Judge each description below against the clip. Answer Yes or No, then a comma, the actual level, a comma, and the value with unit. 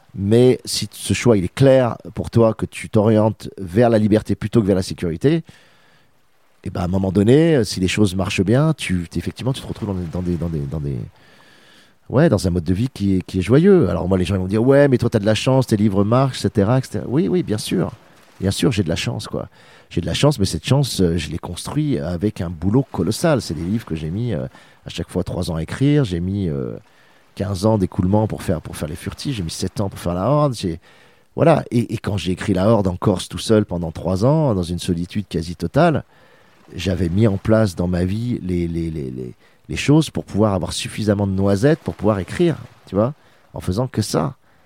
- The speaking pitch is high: No, low, 100 Hz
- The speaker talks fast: Yes, fast, 250 wpm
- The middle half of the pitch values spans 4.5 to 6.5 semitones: Yes, average, 4.9 semitones